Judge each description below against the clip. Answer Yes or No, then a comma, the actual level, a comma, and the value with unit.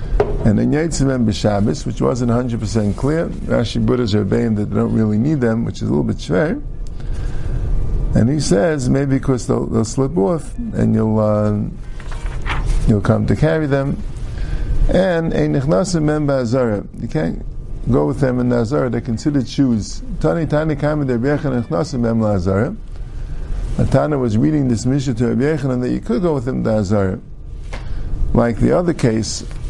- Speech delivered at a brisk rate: No, average, 145 wpm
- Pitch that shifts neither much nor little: Yes, average, 4.0 semitones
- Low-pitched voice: Yes, low, 120 Hz